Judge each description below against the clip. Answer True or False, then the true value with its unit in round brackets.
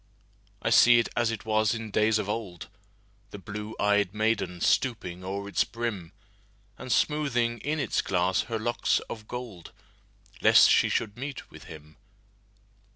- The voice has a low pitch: True (105 Hz)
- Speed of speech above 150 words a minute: False (140 wpm)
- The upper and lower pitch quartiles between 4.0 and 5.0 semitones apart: False (2.8 semitones)